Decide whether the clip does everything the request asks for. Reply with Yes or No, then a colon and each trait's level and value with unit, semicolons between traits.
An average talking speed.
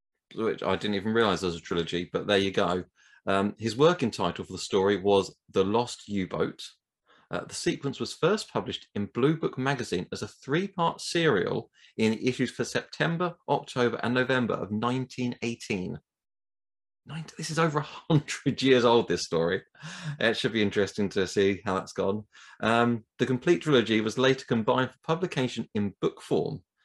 Yes: average, 170 wpm